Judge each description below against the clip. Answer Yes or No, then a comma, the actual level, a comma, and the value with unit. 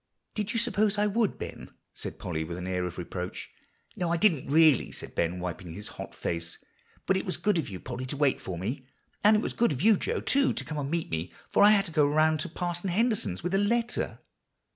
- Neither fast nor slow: No, fast, 240 wpm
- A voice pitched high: No, medium, 155 Hz